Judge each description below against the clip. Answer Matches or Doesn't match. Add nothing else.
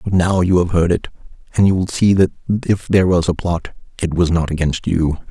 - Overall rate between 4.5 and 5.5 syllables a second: Doesn't match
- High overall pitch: Doesn't match